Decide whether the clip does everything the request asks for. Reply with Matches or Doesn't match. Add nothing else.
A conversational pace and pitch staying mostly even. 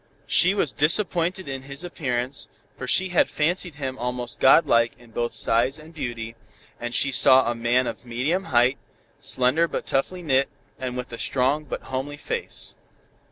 Doesn't match